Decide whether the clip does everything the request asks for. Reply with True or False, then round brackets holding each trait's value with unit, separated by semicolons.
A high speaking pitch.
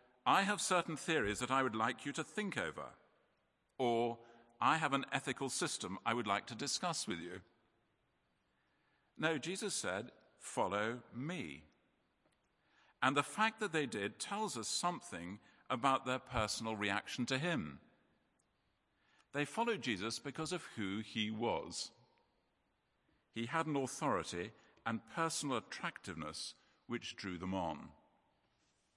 False (130 Hz)